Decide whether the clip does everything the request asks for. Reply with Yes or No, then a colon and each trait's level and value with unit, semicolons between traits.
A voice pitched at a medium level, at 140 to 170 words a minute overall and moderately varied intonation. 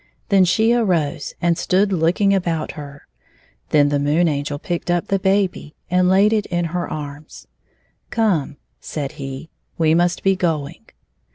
Yes: medium, 170 Hz; average, 160 wpm; average, 4.3 semitones